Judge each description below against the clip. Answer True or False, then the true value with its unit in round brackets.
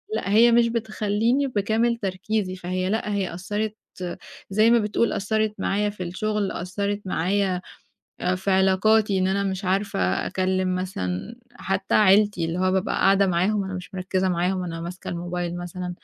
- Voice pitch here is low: False (195 Hz)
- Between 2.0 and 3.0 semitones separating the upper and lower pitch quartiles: True (2.4 semitones)